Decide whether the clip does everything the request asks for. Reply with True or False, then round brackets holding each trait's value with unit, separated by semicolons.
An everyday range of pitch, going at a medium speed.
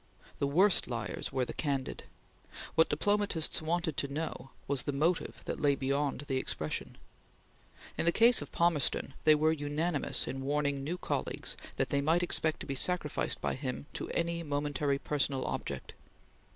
True (3.2 semitones; 165 wpm)